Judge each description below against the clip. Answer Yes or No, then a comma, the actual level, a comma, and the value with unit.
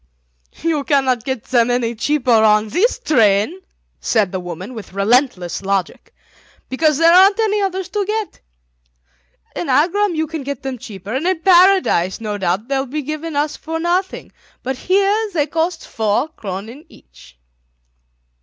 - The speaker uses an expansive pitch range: Yes, wide, 8.0 semitones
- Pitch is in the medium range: No, very high, 275 Hz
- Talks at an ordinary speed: Yes, average, 160 wpm